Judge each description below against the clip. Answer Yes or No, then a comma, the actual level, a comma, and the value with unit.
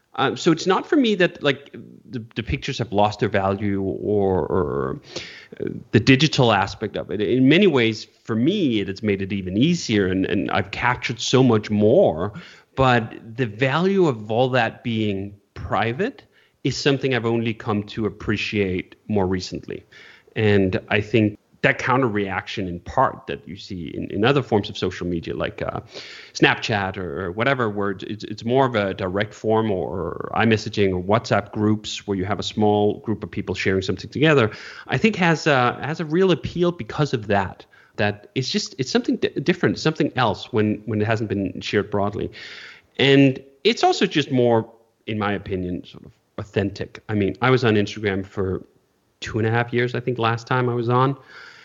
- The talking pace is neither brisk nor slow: Yes, average, 195 wpm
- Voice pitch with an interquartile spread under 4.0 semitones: No, average, 4.3 semitones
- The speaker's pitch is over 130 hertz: No, low, 110 Hz